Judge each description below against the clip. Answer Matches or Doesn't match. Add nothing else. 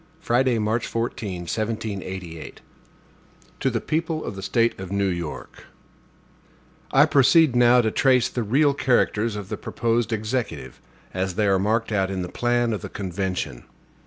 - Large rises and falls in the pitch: Doesn't match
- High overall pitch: Doesn't match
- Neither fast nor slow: Matches